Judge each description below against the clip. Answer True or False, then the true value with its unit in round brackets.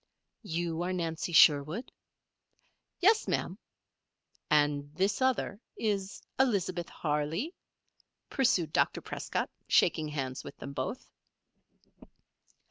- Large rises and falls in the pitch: True (5.7 semitones)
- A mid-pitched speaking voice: True (170 Hz)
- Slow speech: True (95 wpm)